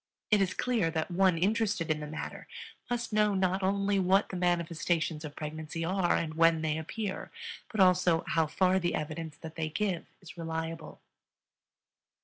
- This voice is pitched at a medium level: Yes, medium, 175 Hz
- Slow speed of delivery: No, average, 165 wpm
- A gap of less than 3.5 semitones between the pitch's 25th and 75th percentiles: Yes, average, 3.1 semitones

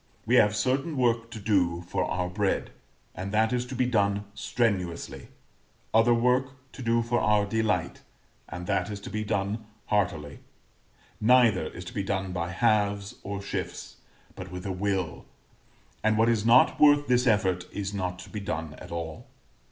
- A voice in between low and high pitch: No, low, 105 Hz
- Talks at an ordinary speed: Yes, average, 175 wpm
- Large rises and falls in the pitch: No, average, 3.9 semitones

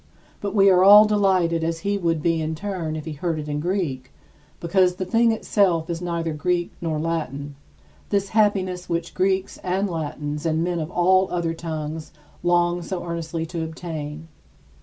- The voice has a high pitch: No, medium, 170 Hz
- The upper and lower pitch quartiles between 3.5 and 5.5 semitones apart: No, average, 2.7 semitones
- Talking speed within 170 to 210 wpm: Yes, average, 180 wpm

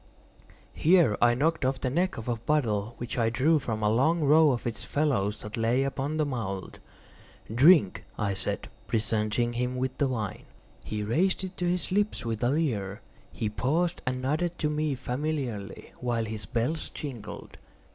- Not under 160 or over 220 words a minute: Yes, average, 170 wpm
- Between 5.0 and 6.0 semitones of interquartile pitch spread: Yes, wide, 5.4 semitones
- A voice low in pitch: Yes, low, 125 Hz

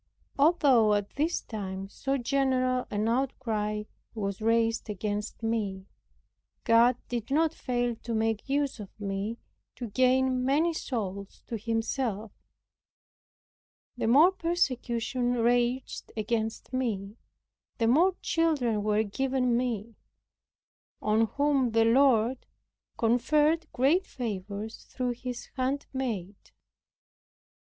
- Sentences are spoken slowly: Yes, slow, 105 wpm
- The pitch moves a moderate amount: Yes, average, 3.5 semitones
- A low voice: No, high, 240 Hz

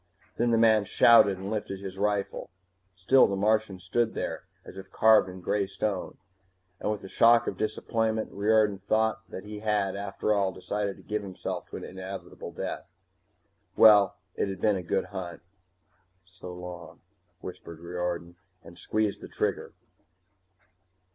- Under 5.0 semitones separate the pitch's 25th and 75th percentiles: Yes, narrow, 2.5 semitones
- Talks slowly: No, average, 155 wpm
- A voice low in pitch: Yes, low, 100 Hz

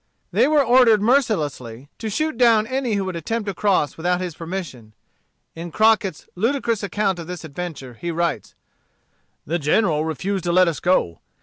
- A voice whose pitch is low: No, medium, 185 Hz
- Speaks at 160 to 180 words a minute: Yes, average, 170 wpm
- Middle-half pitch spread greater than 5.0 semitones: Yes, wide, 5.4 semitones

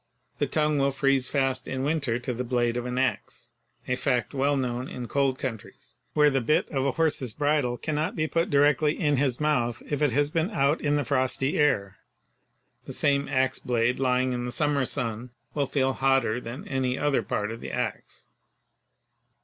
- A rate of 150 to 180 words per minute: No, average, 190 wpm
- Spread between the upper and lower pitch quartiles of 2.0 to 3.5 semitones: Yes, average, 2.8 semitones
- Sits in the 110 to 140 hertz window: Yes, low, 135 Hz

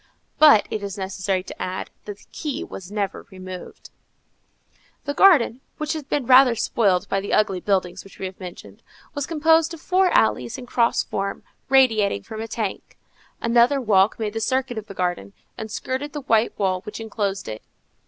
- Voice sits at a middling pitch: No, high, 215 Hz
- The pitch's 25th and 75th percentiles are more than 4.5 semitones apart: Yes, wide, 5.5 semitones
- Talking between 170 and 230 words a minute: Yes, average, 185 wpm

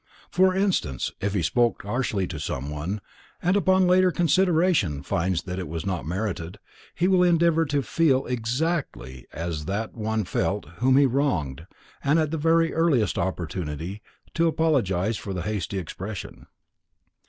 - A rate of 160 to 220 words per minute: No, average, 145 wpm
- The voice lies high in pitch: No, low, 110 Hz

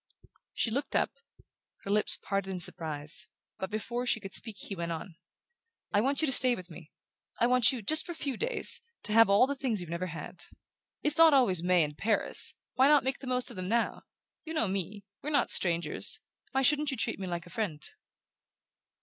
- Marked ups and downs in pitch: Yes, wide, 6.4 semitones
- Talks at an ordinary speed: No, fast, 210 wpm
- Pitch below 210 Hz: No, high, 215 Hz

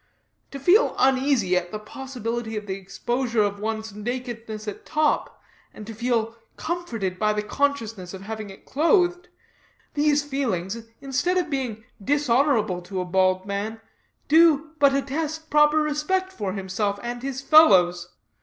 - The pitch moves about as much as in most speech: No, wide, 6.0 semitones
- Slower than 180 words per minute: Yes, average, 155 wpm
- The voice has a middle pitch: No, high, 235 Hz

